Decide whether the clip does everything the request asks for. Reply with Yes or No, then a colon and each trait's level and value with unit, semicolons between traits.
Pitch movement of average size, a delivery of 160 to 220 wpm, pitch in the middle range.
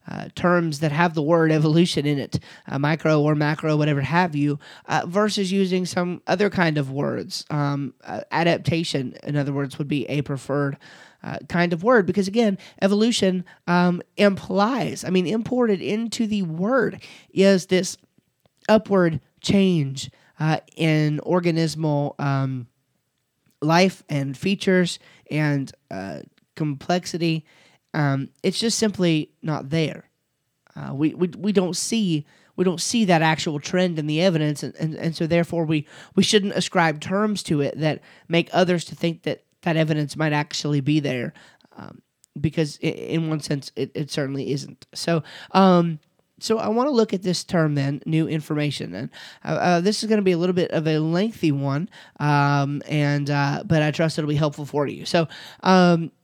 Yes: average, 3.8 semitones; average, 170 wpm; medium, 165 Hz